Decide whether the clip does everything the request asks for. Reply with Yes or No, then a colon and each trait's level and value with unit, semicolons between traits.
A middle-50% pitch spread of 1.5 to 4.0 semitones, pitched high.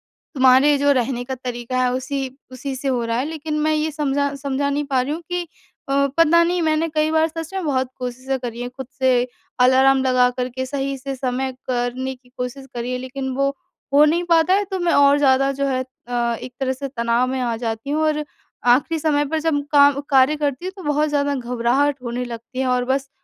Yes: average, 2.8 semitones; very high, 270 Hz